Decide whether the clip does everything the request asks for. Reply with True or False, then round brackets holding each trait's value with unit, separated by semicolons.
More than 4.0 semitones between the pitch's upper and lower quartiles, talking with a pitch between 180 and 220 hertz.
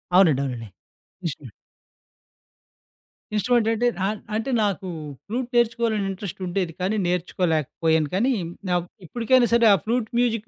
True (5.1 semitones; 200 Hz)